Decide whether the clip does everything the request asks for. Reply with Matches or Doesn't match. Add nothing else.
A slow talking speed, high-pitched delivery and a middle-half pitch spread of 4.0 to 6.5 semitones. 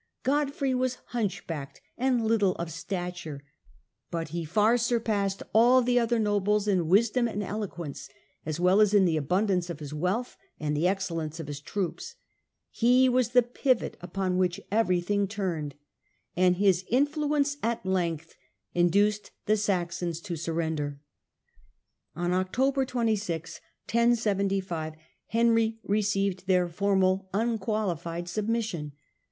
Matches